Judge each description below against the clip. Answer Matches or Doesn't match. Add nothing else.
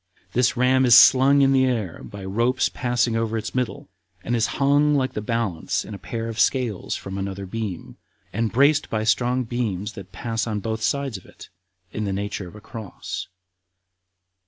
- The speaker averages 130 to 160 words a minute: Doesn't match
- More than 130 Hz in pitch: Doesn't match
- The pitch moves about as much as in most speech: Matches